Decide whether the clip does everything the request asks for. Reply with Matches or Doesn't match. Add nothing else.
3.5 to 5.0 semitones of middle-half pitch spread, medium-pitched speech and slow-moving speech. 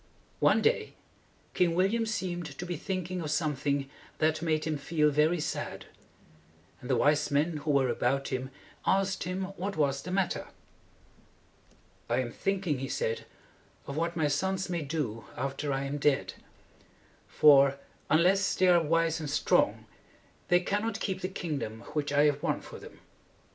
Doesn't match